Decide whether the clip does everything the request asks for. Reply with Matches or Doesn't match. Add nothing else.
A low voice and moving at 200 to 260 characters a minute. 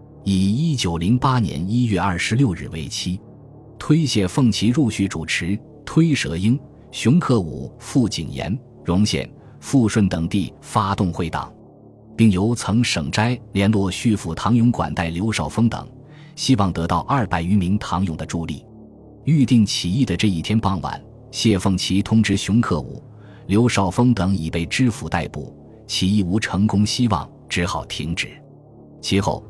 Matches